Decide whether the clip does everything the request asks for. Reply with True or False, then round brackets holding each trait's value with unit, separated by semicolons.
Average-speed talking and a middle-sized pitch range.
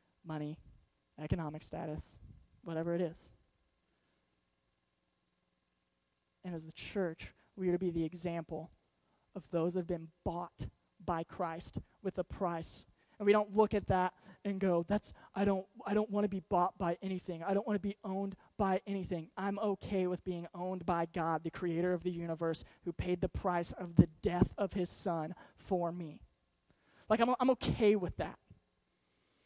True (170 wpm; 3.1 semitones)